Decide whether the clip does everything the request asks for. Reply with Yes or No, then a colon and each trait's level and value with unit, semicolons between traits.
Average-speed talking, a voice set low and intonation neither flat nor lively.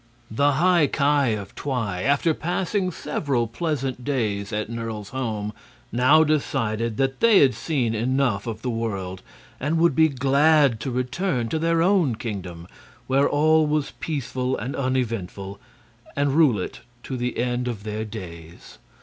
Yes: average, 150 wpm; low, 130 Hz; average, 5.0 semitones